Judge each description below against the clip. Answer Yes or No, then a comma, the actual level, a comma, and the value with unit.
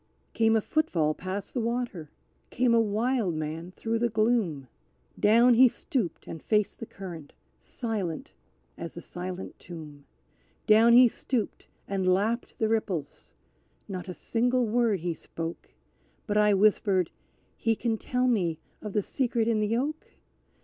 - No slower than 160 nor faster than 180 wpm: No, average, 150 wpm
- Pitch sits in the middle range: No, high, 215 Hz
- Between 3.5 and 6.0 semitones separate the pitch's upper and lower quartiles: Yes, average, 4.6 semitones